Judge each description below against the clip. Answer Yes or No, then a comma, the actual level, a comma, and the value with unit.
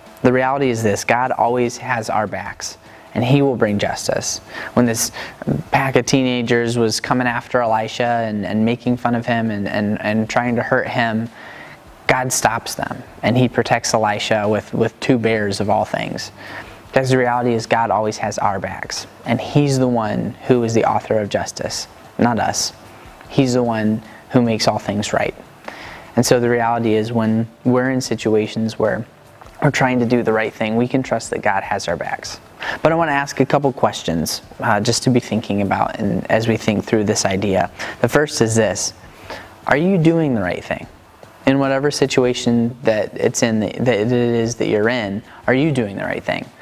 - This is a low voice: Yes, low, 120 Hz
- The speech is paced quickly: No, average, 195 wpm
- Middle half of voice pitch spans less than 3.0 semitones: Yes, narrow, 2.5 semitones